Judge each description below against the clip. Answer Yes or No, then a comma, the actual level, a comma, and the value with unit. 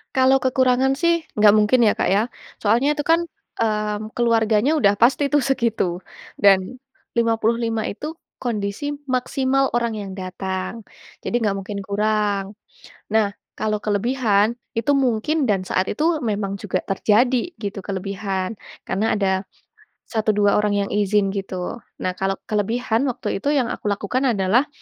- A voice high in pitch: Yes, high, 215 Hz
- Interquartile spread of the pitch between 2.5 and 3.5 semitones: No, average, 4.0 semitones